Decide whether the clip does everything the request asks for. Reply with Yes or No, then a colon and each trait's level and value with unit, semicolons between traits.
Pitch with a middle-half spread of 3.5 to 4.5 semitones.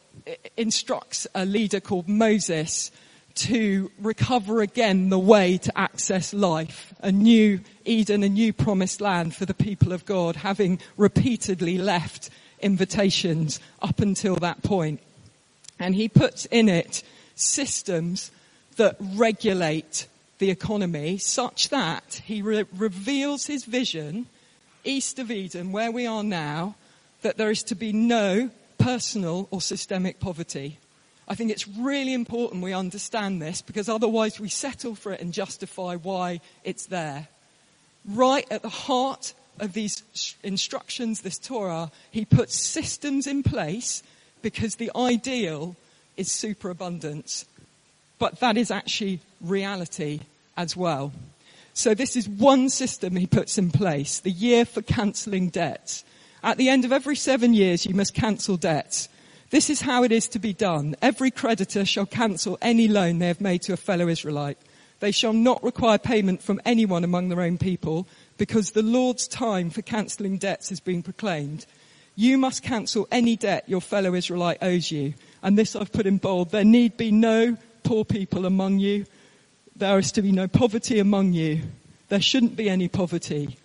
Yes: average, 4.1 semitones